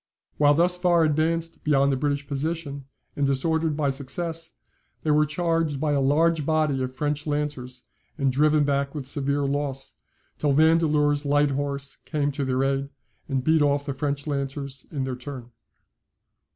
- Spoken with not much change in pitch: Yes, narrow, 1.9 semitones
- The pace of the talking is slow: No, average, 165 wpm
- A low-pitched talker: No, medium, 145 Hz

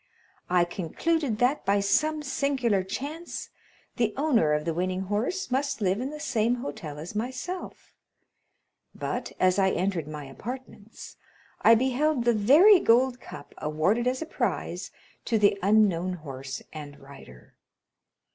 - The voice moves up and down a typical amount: No, wide, 6.5 semitones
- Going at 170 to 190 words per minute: No, average, 140 wpm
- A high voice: Yes, high, 215 Hz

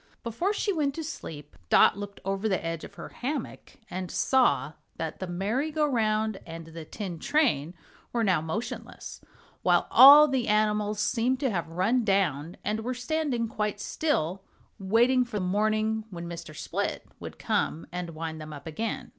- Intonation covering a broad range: Yes, wide, 6.4 semitones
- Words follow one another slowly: No, average, 170 wpm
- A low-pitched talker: No, high, 210 Hz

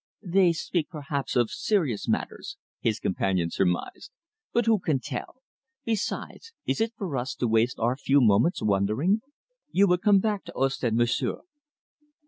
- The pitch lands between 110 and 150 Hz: Yes, medium, 140 Hz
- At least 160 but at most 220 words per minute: No, average, 150 wpm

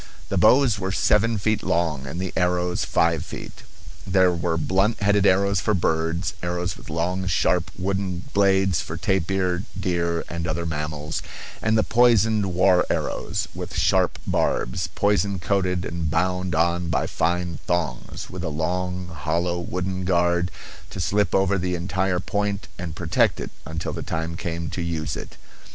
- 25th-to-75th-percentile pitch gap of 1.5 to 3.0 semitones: Yes, narrow, 2.4 semitones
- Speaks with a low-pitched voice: Yes, very low, 90 Hz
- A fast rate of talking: No, average, 160 wpm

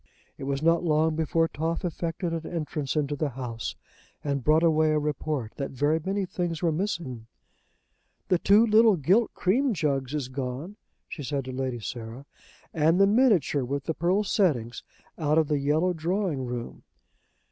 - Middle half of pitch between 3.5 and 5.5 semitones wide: Yes, average, 4.2 semitones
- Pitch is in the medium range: Yes, medium, 155 Hz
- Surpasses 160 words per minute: Yes, average, 170 wpm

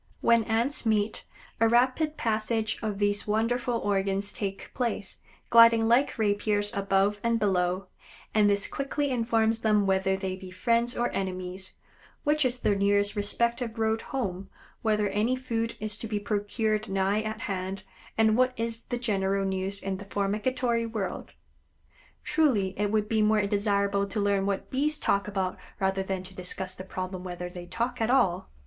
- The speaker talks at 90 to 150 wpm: No, average, 165 wpm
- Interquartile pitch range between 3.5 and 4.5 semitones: No, average, 2.9 semitones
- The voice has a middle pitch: No, high, 210 Hz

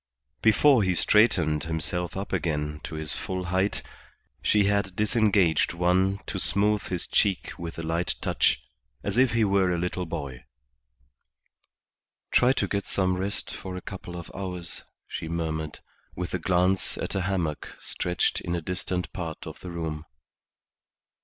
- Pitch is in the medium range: No, very low, 90 Hz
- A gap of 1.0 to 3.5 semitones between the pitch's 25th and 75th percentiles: Yes, average, 2.9 semitones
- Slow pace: No, average, 155 wpm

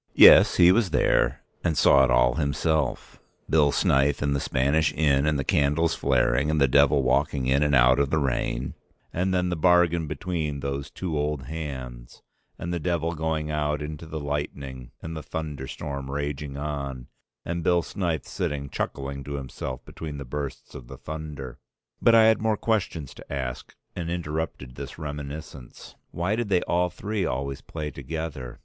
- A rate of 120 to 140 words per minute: No, average, 175 wpm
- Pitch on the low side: Yes, very low, 75 Hz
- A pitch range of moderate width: Yes, average, 3.0 semitones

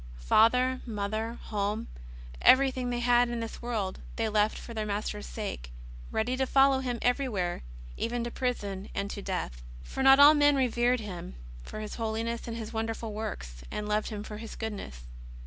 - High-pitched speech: Yes, high, 225 Hz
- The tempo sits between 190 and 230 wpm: No, average, 170 wpm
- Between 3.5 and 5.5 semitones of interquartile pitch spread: No, average, 2.9 semitones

